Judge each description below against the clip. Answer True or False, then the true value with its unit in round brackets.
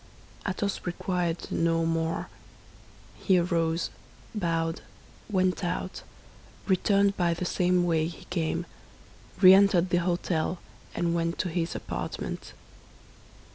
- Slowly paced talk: True (110 wpm)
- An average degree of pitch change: False (1.9 semitones)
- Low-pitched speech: False (175 Hz)